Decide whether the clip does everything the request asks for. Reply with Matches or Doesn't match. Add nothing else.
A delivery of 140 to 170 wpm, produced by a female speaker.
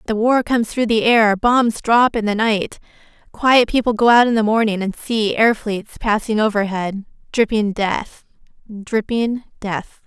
Matches